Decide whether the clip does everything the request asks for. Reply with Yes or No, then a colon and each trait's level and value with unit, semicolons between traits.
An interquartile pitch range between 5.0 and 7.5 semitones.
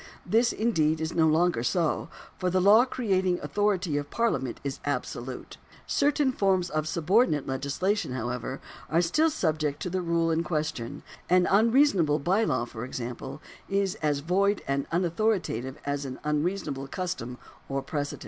Yes: wide, 5.6 semitones